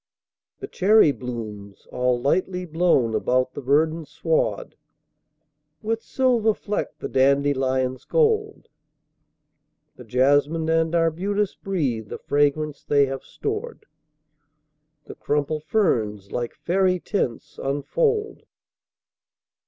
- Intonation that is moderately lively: No, wide, 6.9 semitones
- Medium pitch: Yes, medium, 150 Hz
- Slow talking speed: Yes, slow, 100 wpm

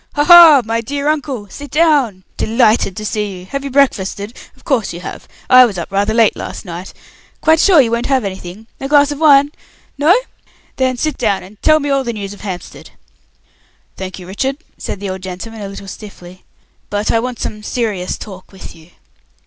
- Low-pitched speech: No, high, 225 Hz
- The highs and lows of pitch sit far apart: Yes, wide, 6.1 semitones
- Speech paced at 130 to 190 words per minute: No, average, 200 wpm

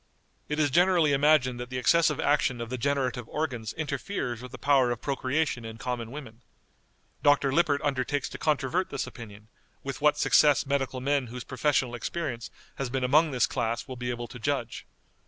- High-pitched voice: No, low, 135 Hz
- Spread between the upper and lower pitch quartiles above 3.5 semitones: No, average, 3.0 semitones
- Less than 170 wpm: No, average, 180 wpm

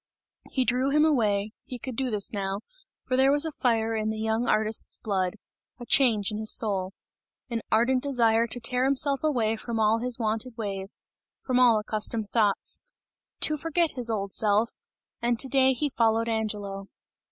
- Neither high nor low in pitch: No, high, 230 Hz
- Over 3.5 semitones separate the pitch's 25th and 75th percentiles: No, average, 3.1 semitones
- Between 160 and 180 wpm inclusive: Yes, average, 175 wpm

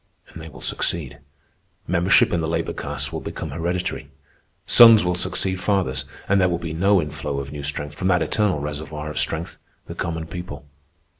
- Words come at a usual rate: Yes, average, 180 wpm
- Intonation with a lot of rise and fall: No, average, 3.5 semitones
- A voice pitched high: No, very low, 85 Hz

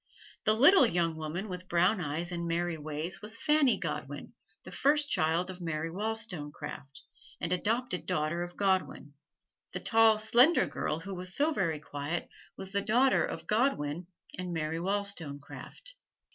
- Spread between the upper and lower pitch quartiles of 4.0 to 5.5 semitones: Yes, average, 5.2 semitones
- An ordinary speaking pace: Yes, average, 150 wpm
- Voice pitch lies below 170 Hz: No, medium, 180 Hz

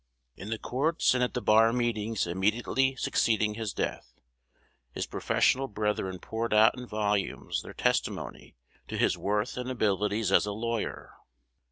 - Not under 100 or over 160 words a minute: Yes, average, 150 wpm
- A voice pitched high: No, low, 110 Hz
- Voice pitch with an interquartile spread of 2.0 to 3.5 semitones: Yes, narrow, 2.6 semitones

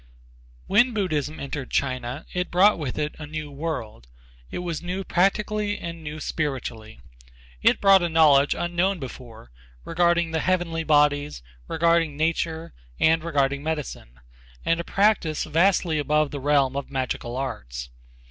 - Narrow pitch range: No, average, 3.6 semitones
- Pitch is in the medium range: Yes, medium, 155 Hz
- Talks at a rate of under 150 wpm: Yes, average, 140 wpm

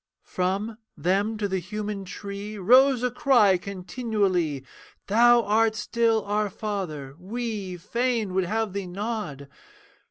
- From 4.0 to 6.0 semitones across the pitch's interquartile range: No, average, 3.3 semitones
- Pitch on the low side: No, high, 205 Hz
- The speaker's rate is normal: No, slow, 125 wpm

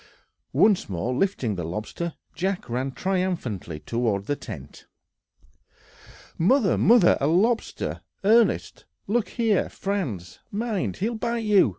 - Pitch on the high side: No, medium, 180 Hz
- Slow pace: Yes, slow, 115 wpm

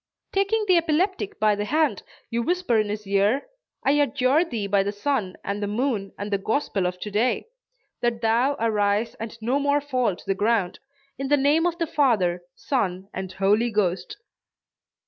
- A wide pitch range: Yes, wide, 6.0 semitones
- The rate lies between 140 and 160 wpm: No, average, 185 wpm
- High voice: Yes, high, 230 Hz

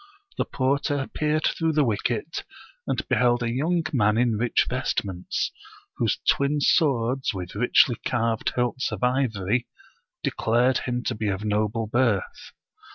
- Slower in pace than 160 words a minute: Yes, average, 140 wpm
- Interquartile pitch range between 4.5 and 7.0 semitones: No, average, 3.6 semitones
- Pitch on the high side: No, low, 120 Hz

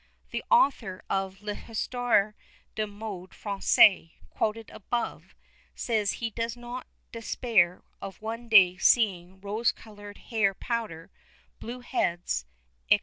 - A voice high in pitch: Yes, high, 215 Hz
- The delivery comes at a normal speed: No, slow, 115 wpm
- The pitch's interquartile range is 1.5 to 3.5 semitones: Yes, average, 3.2 semitones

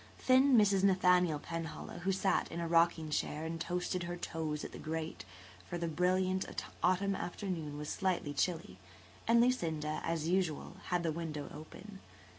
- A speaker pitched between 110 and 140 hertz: No, medium, 170 Hz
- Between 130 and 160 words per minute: Yes, average, 155 wpm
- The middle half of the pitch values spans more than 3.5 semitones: No, average, 2.9 semitones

